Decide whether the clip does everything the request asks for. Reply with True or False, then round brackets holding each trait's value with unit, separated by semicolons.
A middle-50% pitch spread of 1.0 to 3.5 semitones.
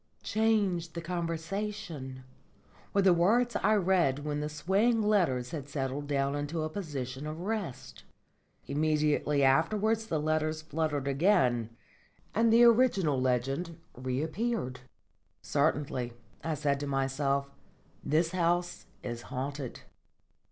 False (5.5 semitones)